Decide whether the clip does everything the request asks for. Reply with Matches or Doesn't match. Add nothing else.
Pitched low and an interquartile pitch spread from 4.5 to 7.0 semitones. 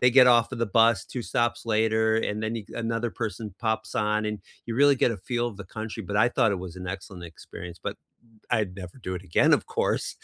Doesn't match